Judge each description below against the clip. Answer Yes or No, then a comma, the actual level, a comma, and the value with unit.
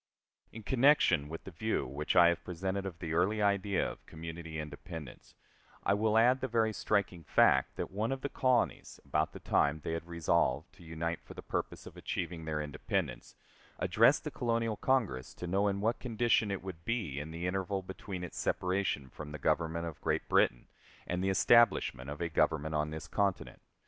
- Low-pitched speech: Yes, very low, 90 Hz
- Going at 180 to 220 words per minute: Yes, average, 190 wpm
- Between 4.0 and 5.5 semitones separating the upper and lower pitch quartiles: Yes, average, 4.6 semitones